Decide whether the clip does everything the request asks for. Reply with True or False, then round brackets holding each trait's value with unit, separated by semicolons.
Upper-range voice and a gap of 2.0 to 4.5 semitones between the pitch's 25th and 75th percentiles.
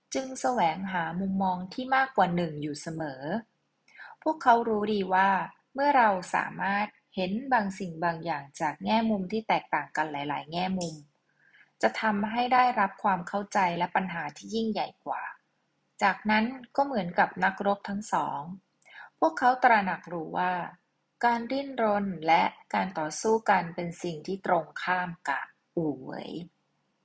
True (195 Hz; 4.2 semitones)